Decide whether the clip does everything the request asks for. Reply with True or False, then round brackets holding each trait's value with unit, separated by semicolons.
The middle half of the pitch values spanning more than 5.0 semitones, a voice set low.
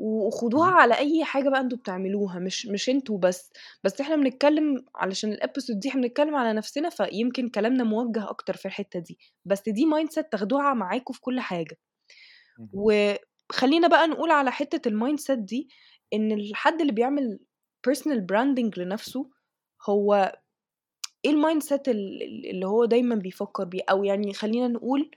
False (5.4 semitones; 235 Hz)